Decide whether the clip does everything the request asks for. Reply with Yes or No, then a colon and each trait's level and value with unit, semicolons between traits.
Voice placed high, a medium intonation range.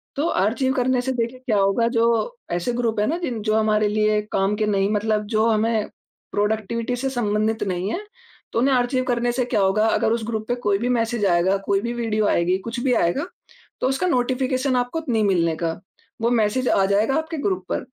Yes: high, 225 Hz; average, 3.1 semitones